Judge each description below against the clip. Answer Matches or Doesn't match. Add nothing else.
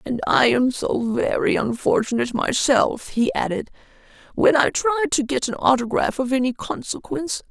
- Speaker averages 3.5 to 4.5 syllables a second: Doesn't match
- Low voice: Doesn't match